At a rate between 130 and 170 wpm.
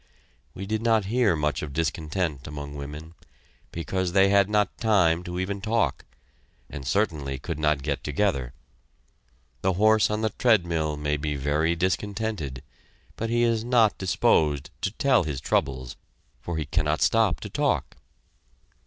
Yes: average, 150 wpm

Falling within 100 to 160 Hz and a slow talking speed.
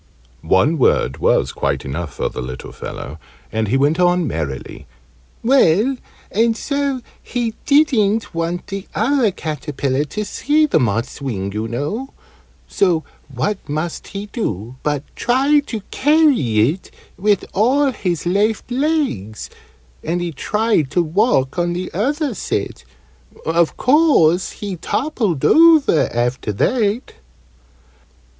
No: medium, 180 Hz; slow, 130 wpm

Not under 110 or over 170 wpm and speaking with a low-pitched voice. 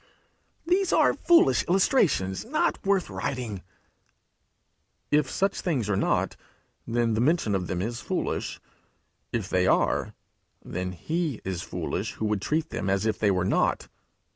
Yes: average, 145 wpm; low, 115 Hz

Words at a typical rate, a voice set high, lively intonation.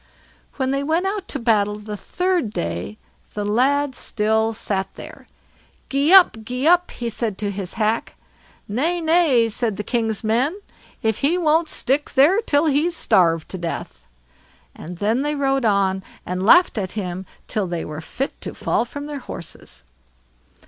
Yes: average, 165 wpm; high, 235 Hz; wide, 6.2 semitones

